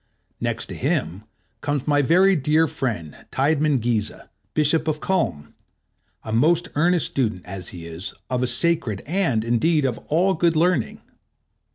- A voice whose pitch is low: No, medium, 145 Hz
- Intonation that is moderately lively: No, wide, 6.5 semitones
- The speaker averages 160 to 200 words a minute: No, average, 145 wpm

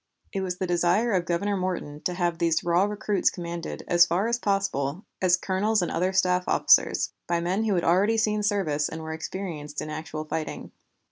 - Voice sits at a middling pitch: Yes, medium, 180 Hz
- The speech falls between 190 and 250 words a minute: Yes, average, 195 wpm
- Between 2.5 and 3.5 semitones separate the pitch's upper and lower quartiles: Yes, average, 2.9 semitones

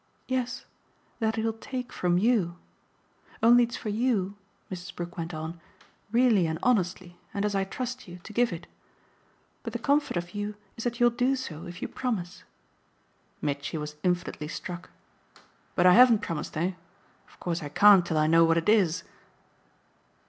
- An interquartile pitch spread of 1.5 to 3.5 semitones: No, wide, 5.4 semitones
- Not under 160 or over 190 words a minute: Yes, average, 170 wpm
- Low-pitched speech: No, high, 190 Hz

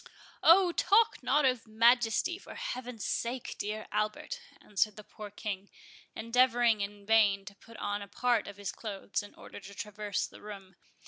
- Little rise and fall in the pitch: No, average, 3.0 semitones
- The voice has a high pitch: Yes, high, 215 Hz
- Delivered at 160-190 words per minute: Yes, average, 170 wpm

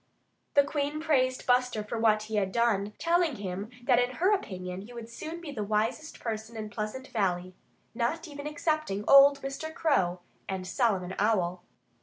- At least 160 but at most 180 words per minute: Yes, average, 170 wpm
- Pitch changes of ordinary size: No, wide, 5.7 semitones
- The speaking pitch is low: No, high, 235 Hz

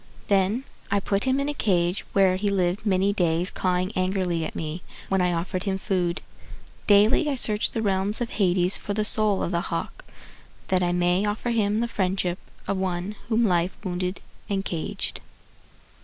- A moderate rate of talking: Yes, average, 180 wpm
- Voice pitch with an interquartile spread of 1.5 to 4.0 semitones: Yes, narrow, 2.6 semitones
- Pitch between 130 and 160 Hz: No, high, 190 Hz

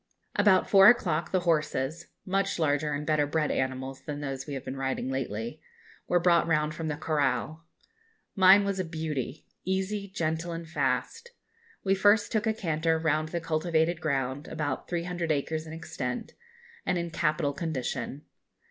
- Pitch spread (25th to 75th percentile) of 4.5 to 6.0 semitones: No, average, 3.3 semitones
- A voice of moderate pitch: Yes, medium, 160 Hz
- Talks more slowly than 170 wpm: Yes, average, 160 wpm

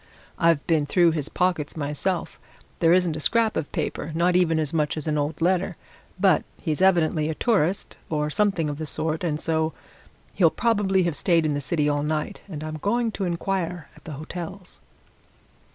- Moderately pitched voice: Yes, medium, 165 Hz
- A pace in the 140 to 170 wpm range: No, average, 185 wpm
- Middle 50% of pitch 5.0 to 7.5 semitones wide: No, average, 3.2 semitones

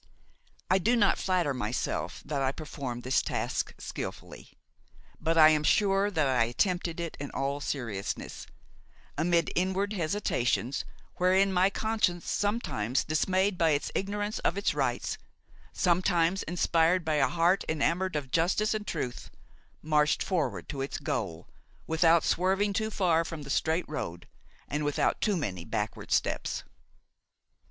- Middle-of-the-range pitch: Yes, medium, 165 Hz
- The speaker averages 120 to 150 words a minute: Yes, average, 140 wpm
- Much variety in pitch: No, average, 4.7 semitones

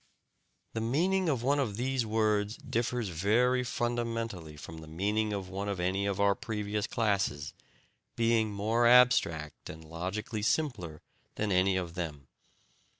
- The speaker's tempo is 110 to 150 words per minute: Yes, average, 145 wpm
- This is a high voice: No, low, 105 Hz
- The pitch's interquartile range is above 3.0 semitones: Yes, average, 4.3 semitones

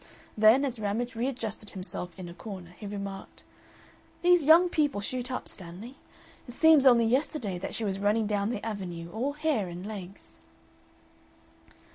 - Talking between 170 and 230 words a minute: No, average, 155 wpm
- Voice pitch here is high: Yes, high, 220 Hz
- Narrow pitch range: No, average, 4.8 semitones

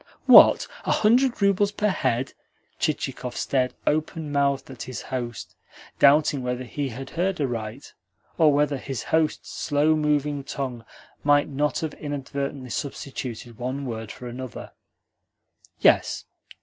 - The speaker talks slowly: Yes, slow, 130 wpm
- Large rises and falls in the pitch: No, average, 2.9 semitones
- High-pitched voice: No, medium, 140 Hz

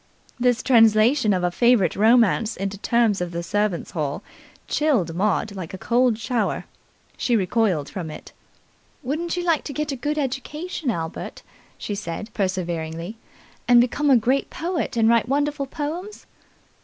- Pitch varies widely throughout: Yes, wide, 6.3 semitones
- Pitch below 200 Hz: No, high, 230 Hz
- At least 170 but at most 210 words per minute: No, average, 155 wpm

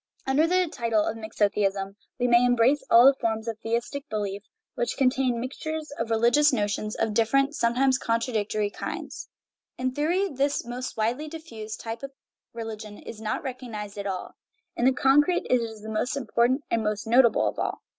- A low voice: No, high, 235 Hz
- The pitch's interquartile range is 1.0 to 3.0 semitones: No, average, 3.6 semitones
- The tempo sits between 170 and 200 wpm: Yes, average, 175 wpm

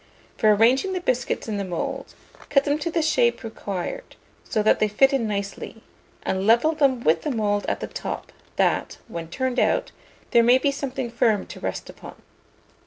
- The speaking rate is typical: Yes, average, 185 wpm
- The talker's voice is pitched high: Yes, high, 235 Hz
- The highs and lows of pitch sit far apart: No, average, 4.9 semitones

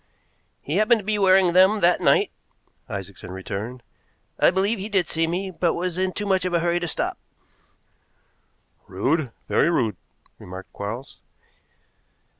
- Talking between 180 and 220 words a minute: No, average, 150 wpm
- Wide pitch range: Yes, wide, 7.0 semitones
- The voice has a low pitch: No, medium, 175 Hz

